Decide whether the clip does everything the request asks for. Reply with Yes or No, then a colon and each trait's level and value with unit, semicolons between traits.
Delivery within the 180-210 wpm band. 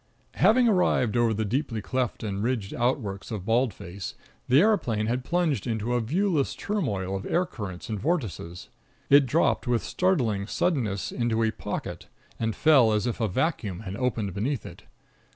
No: average, 170 wpm